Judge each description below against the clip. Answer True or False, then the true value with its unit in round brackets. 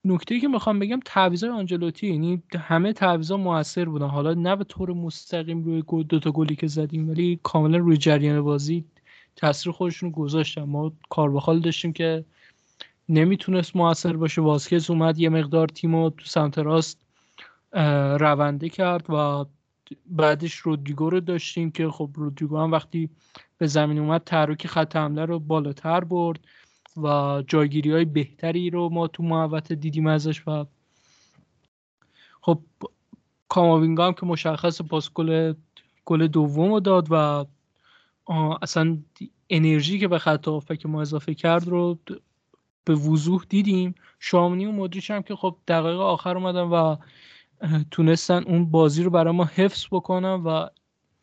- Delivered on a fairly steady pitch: True (2.1 semitones)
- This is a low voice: False (165 Hz)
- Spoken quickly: False (145 wpm)